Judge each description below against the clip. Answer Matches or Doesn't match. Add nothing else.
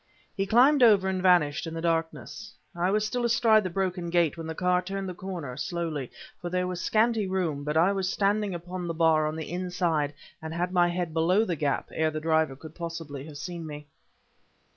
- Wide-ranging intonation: Doesn't match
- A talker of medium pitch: Matches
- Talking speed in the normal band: Doesn't match